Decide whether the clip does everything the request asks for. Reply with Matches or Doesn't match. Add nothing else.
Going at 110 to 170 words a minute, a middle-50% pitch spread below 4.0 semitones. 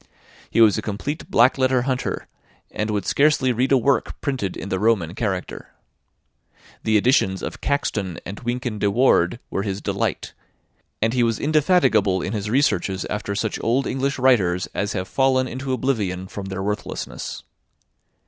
Doesn't match